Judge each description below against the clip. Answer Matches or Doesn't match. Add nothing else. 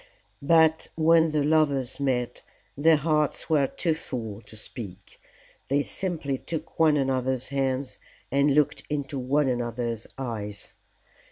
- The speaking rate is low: Matches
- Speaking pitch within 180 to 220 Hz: Doesn't match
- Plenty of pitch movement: Doesn't match